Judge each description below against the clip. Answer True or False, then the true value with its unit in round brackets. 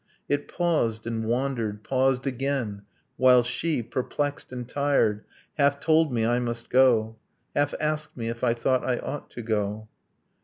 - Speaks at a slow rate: False (155 wpm)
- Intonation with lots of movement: False (3.6 semitones)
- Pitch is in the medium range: False (125 Hz)